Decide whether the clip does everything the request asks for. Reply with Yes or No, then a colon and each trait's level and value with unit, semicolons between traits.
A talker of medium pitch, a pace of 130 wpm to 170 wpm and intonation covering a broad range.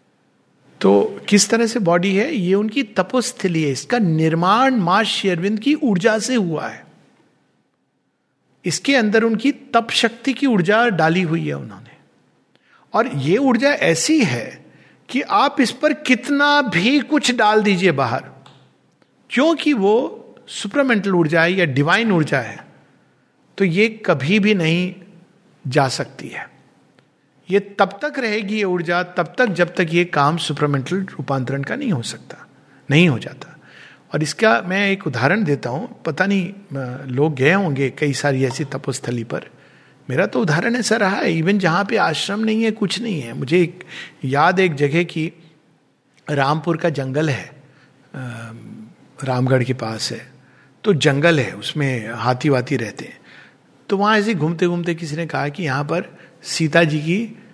Yes: medium, 175 Hz; average, 155 wpm; wide, 6.8 semitones